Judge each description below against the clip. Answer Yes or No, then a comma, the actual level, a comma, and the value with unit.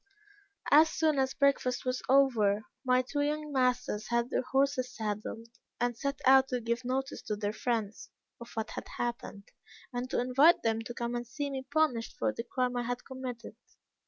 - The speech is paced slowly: No, average, 185 wpm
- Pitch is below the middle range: No, very high, 250 Hz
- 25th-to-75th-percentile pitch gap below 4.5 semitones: Yes, narrow, 2.4 semitones